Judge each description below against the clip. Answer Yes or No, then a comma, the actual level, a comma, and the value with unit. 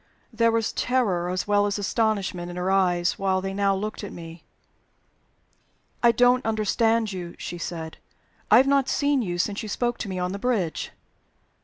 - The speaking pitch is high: Yes, high, 200 Hz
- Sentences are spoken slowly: No, average, 180 wpm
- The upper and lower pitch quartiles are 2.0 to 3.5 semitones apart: No, average, 4.1 semitones